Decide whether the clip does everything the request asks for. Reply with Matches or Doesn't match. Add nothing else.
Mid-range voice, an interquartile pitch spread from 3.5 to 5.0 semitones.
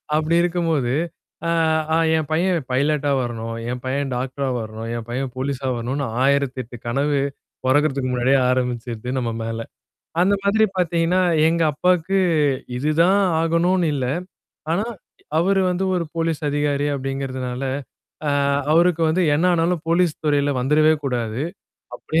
Matches